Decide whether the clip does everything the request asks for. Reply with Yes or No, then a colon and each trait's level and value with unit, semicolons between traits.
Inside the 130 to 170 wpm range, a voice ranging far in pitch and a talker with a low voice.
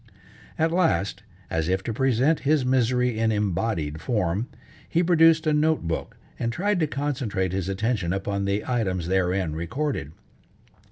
Yes: average, 150 wpm; wide, 7.6 semitones; low, 115 Hz